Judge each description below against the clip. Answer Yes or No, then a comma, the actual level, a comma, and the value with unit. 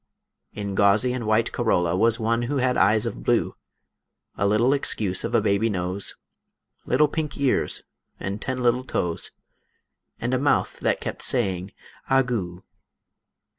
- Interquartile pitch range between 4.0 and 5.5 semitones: Yes, average, 4.3 semitones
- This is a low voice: Yes, low, 110 Hz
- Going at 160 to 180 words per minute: No, average, 150 wpm